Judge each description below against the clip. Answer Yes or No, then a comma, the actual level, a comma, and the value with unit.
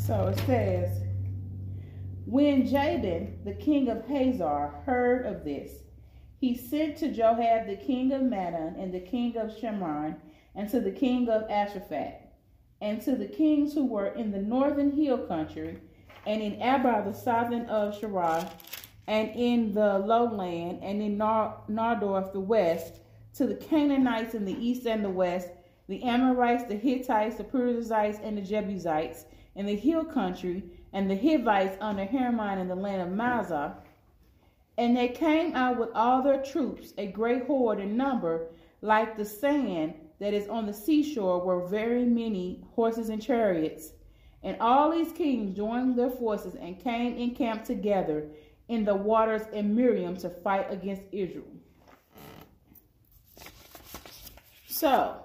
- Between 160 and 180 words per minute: No, average, 150 wpm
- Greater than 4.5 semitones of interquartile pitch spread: Yes, average, 4.9 semitones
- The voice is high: Yes, high, 215 Hz